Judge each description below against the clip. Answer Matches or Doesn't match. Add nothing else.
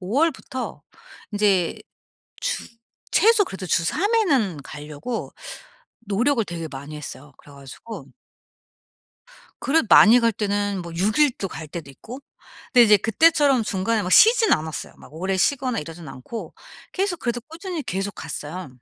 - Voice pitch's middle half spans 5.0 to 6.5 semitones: Doesn't match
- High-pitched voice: Matches